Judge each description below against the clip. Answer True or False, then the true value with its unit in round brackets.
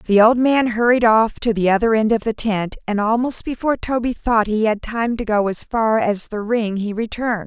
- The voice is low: False (220 Hz)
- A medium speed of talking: False (235 wpm)